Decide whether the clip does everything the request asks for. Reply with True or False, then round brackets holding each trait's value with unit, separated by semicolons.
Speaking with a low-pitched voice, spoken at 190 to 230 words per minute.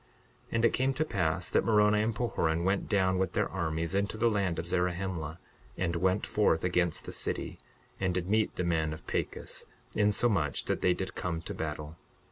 True (90 Hz; 195 wpm)